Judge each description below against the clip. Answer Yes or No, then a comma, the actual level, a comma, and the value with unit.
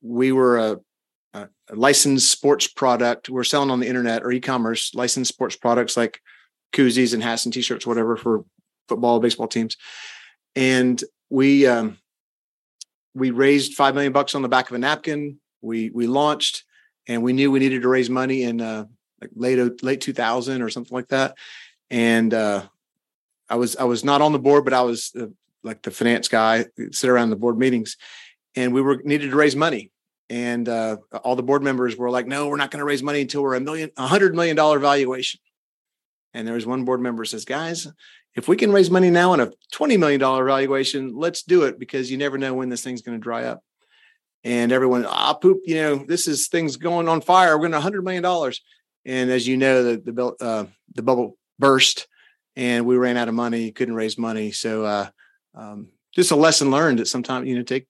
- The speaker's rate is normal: No, fast, 210 wpm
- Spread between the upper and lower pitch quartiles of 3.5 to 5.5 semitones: No, average, 3.0 semitones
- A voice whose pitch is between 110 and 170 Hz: Yes, low, 130 Hz